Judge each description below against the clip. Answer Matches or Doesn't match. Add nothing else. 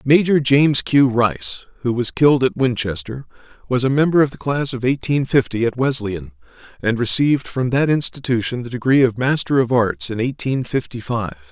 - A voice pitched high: Doesn't match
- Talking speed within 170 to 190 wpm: Matches